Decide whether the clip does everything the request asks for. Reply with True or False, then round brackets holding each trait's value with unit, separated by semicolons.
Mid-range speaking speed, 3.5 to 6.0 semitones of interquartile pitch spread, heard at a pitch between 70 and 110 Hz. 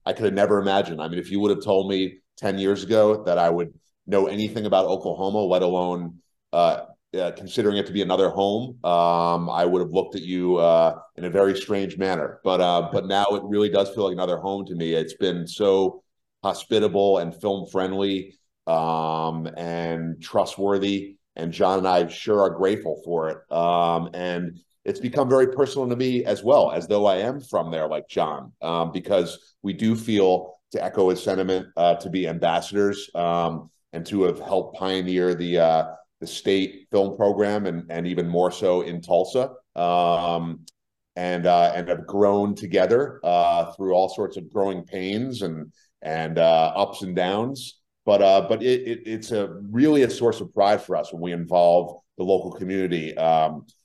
False (190 wpm; 2.6 semitones; 95 Hz)